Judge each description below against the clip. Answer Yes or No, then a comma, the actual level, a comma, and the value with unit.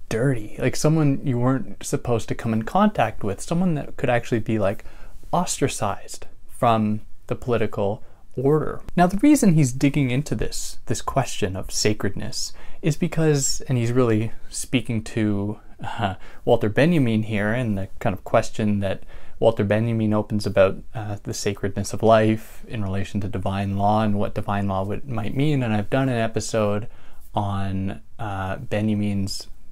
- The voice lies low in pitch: Yes, low, 110 Hz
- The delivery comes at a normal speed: Yes, average, 160 wpm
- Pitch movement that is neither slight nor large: Yes, average, 3.8 semitones